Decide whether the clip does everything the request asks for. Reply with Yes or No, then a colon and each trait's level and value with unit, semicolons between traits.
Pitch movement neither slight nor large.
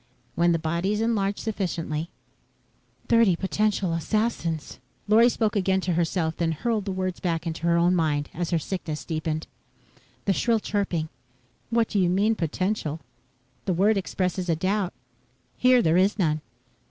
Yes: average, 3.9 semitones